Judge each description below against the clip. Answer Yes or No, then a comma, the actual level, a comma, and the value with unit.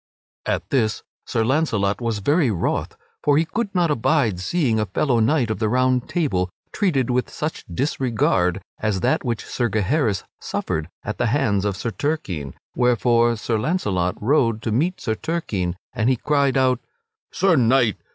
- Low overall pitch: Yes, low, 120 Hz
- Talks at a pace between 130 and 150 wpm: No, average, 165 wpm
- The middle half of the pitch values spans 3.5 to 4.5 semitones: No, average, 5.2 semitones